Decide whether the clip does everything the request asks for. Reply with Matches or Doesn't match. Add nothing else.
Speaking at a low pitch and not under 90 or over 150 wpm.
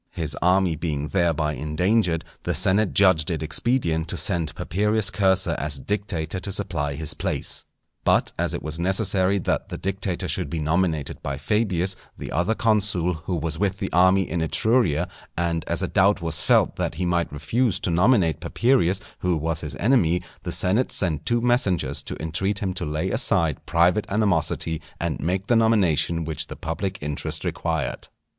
Doesn't match